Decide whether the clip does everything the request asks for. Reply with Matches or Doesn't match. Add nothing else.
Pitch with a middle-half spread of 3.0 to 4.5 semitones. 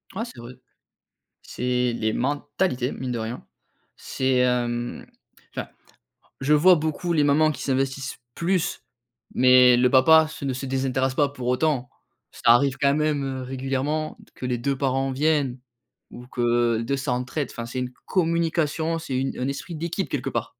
Matches